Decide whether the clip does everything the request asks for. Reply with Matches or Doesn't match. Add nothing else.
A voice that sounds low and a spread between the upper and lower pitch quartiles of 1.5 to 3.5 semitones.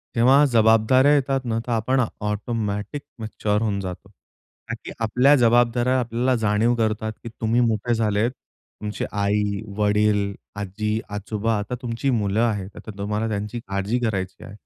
Matches